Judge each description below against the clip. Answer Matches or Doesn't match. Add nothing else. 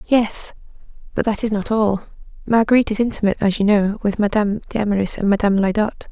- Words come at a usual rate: Matches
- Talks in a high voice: Matches